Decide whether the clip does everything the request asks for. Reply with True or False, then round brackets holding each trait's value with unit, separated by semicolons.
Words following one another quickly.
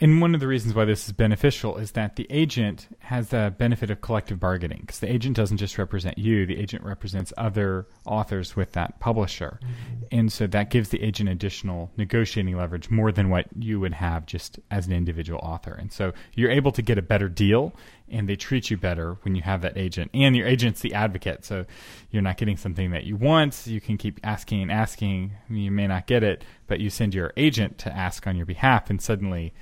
True (220 wpm)